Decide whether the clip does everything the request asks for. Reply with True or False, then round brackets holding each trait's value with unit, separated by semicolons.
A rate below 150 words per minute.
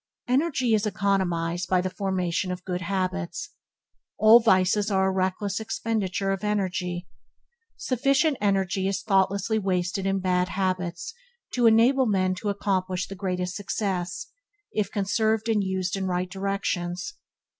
True (135 wpm)